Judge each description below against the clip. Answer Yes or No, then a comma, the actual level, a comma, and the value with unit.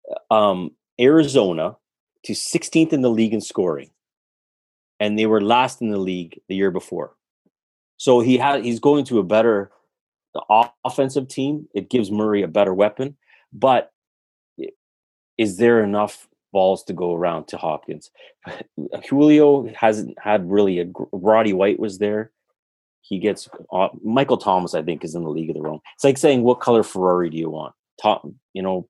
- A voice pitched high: No, low, 110 Hz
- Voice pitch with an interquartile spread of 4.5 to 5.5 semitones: Yes, average, 5.1 semitones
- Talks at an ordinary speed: Yes, average, 170 wpm